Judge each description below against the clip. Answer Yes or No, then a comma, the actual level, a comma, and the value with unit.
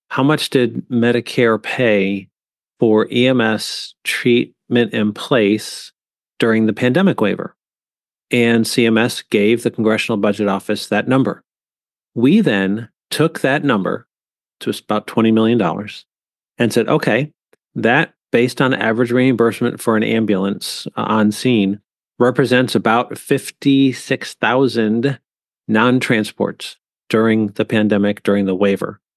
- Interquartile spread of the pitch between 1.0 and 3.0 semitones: Yes, narrow, 2.6 semitones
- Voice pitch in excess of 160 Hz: No, low, 115 Hz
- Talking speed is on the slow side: Yes, slow, 115 wpm